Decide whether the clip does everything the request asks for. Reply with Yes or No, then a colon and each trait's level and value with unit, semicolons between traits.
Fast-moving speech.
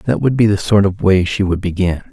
Yes: fast, 285 wpm